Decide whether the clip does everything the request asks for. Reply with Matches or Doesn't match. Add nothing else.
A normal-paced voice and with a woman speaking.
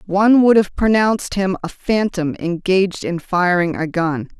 Matches